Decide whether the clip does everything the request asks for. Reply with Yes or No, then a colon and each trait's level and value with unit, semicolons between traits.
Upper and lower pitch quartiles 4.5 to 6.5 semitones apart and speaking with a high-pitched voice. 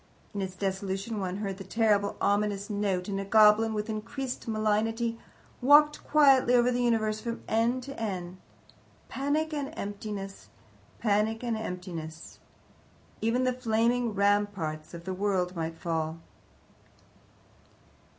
No: average, 3.3 semitones; high, 210 Hz